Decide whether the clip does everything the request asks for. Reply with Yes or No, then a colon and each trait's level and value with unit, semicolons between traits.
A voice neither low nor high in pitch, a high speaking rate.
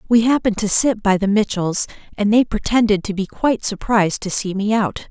No: high, 210 Hz; fast, 210 wpm